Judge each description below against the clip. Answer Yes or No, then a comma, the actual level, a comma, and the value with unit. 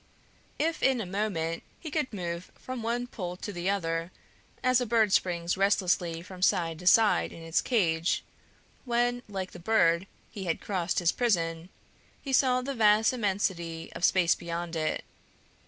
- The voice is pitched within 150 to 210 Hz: Yes, high, 190 Hz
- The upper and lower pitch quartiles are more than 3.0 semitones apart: Yes, average, 5.2 semitones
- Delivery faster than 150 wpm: Yes, average, 165 wpm